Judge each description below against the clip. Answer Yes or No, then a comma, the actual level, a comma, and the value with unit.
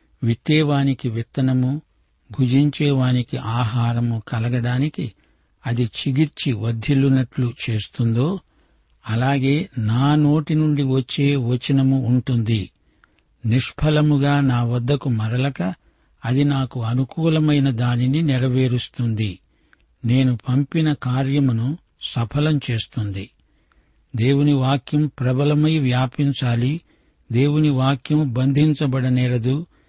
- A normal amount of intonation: Yes, average, 3.0 semitones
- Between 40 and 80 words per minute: Yes, average, 75 wpm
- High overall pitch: No, low, 130 Hz